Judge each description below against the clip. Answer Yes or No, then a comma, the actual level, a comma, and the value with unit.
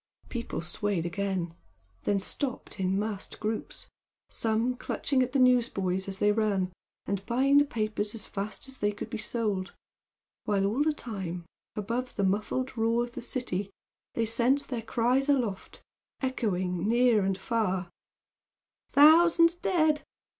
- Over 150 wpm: No, average, 145 wpm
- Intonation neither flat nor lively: Yes, average, 4.4 semitones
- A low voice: No, high, 220 Hz